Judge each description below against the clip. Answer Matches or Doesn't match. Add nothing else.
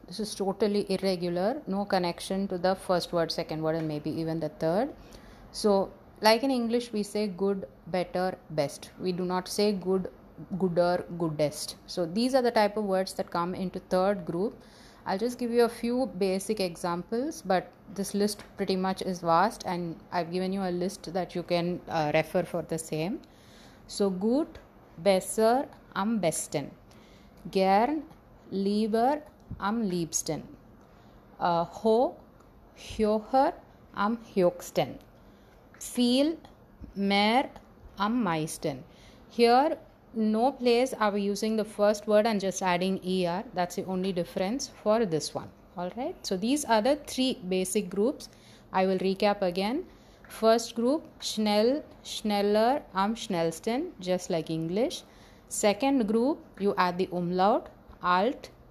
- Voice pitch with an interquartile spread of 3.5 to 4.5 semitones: Matches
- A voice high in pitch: Matches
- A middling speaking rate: Matches